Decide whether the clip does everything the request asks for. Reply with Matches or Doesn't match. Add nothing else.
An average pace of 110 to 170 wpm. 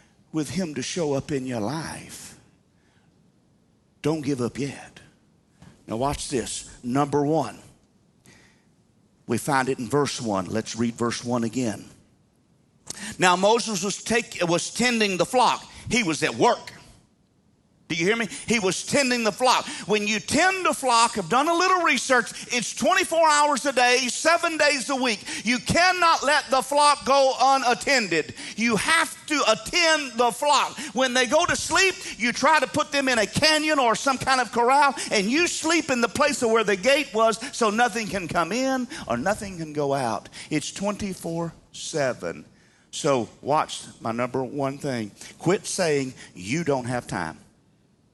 Matches